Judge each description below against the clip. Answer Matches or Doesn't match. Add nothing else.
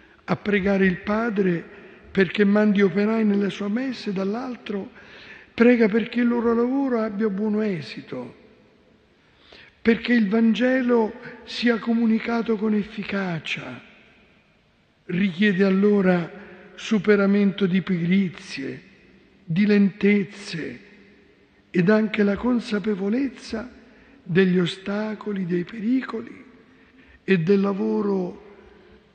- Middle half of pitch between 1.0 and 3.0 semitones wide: Matches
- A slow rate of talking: Matches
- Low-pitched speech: Doesn't match